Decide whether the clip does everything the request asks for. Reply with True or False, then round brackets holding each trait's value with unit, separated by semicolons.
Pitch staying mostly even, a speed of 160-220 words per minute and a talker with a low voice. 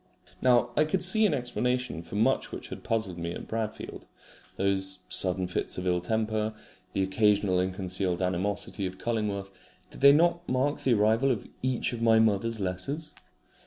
False (4.9 semitones; 170 wpm; 110 Hz)